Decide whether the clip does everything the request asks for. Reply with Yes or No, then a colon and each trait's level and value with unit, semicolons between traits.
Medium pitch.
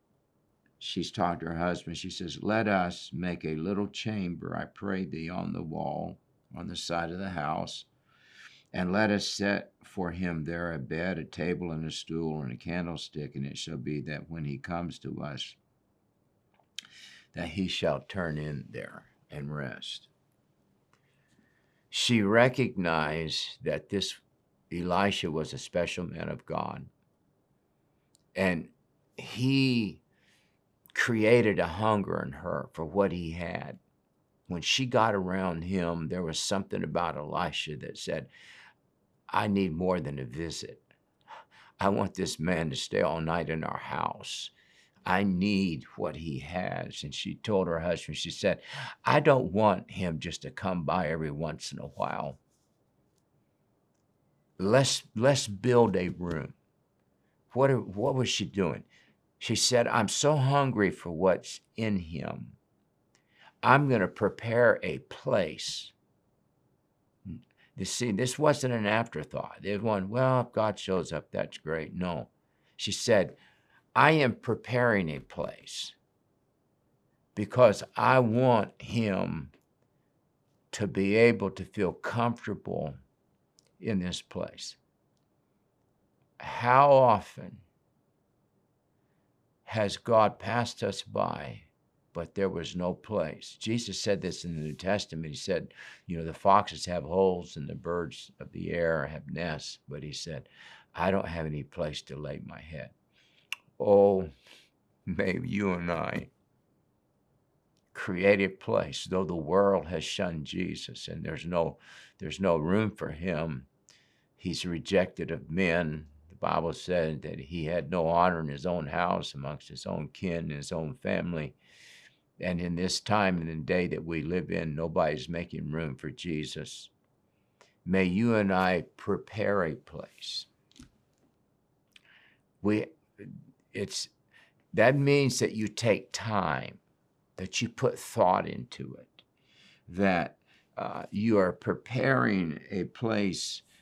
No: very low, 90 Hz